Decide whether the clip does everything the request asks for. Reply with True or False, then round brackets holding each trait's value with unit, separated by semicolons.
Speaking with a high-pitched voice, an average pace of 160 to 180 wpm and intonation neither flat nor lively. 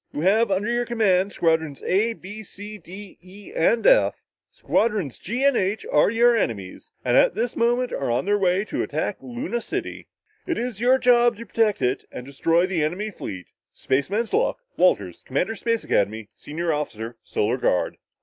False (195 Hz; 175 wpm; 7.6 semitones)